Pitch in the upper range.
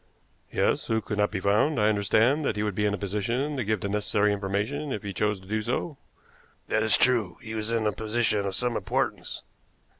No: low, 105 Hz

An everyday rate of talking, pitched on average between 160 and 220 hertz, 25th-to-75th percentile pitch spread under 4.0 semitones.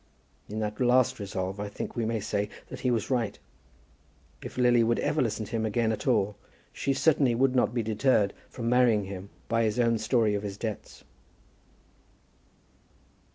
No: average, 175 wpm; low, 115 Hz; average, 2.9 semitones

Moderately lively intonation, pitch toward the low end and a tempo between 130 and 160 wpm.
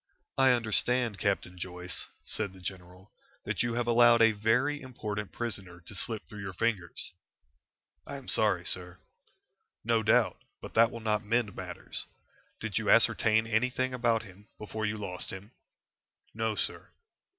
Yes: average, 3.4 semitones; low, 110 Hz; average, 150 wpm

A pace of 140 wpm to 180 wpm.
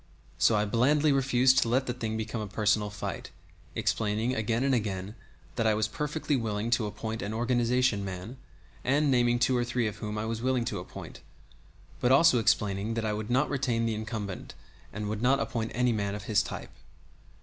No: average, 195 wpm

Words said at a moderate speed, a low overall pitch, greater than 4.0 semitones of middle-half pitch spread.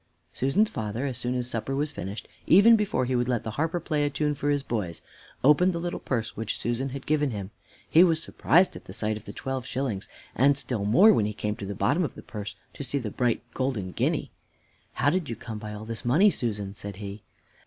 No: fast, 235 wpm; low, 125 Hz; wide, 5.4 semitones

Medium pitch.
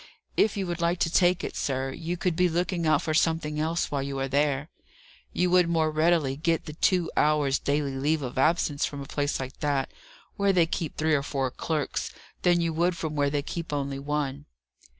Yes: medium, 155 Hz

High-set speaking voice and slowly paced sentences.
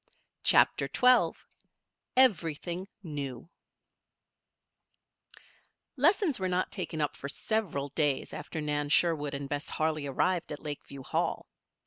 No: medium, 155 Hz; slow, 110 wpm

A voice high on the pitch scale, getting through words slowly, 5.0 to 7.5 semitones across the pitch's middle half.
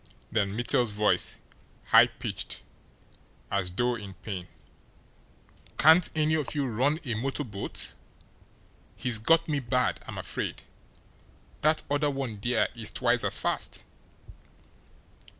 No: low, 120 Hz; slow, 120 wpm; wide, 5.4 semitones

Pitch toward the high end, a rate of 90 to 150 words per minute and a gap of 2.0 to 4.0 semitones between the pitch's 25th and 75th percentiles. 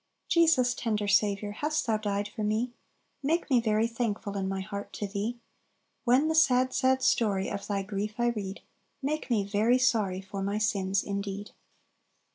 No: high, 215 Hz; average, 170 wpm; average, 3.5 semitones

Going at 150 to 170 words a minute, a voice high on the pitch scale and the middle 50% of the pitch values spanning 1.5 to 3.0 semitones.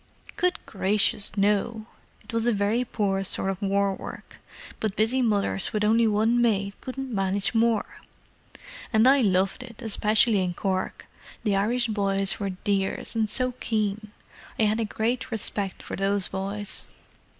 Yes: average, 155 wpm; high, 210 Hz; narrow, 2.6 semitones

